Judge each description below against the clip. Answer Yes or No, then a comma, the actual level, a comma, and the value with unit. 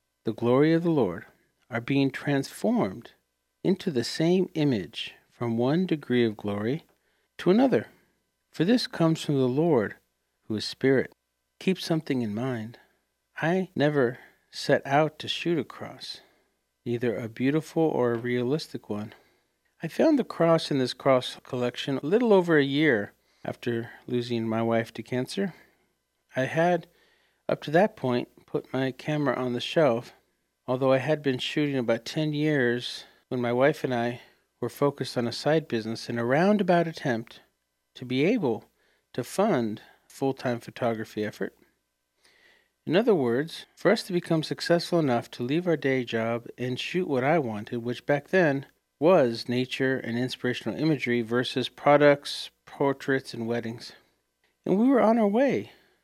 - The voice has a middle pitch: No, low, 130 Hz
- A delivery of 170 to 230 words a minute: No, average, 160 wpm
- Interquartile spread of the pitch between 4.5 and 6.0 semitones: Yes, average, 4.8 semitones